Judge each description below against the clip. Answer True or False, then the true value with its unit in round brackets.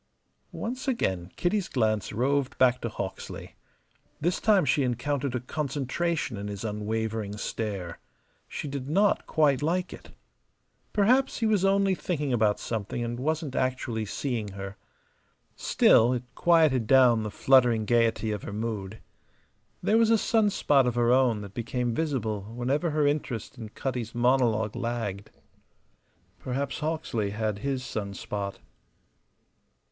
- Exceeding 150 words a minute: False (140 wpm)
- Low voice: True (125 Hz)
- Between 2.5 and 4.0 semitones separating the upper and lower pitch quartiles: False (5.2 semitones)